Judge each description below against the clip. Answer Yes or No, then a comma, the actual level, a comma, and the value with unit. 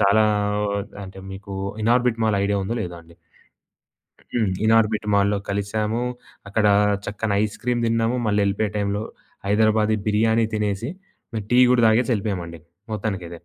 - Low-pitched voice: Yes, low, 105 Hz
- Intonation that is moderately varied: No, narrow, 1.9 semitones